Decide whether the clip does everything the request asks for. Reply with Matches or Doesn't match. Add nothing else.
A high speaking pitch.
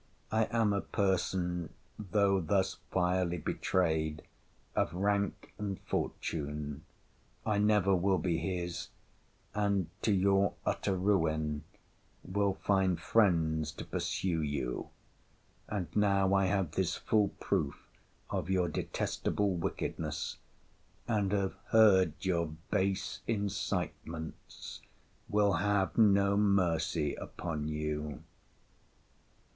Doesn't match